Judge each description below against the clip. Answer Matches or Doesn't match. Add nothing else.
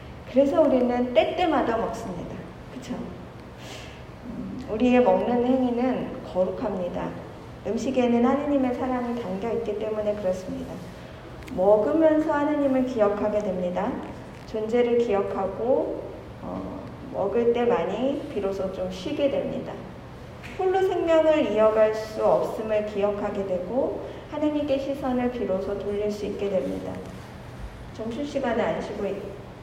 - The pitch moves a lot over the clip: Doesn't match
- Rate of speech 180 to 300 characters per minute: Matches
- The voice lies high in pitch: Matches